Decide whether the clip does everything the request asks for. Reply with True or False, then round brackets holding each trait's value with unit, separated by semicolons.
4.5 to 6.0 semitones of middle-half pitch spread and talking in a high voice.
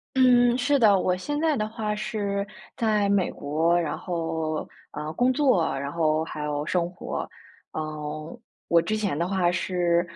False (5.2 semitones; 180 Hz)